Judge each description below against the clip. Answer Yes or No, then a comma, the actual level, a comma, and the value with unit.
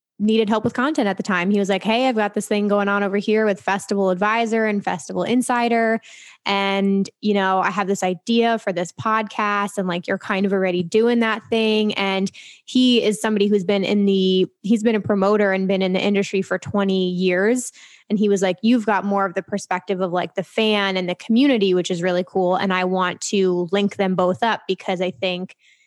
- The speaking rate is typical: No, fast, 225 wpm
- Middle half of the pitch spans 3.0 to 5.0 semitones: No, narrow, 2.5 semitones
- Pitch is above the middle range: Yes, high, 200 Hz